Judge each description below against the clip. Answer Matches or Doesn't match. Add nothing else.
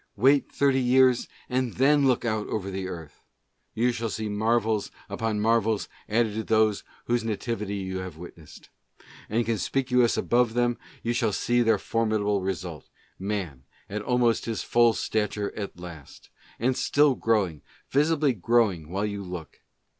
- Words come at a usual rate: Matches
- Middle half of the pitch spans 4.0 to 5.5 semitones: Doesn't match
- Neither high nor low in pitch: Doesn't match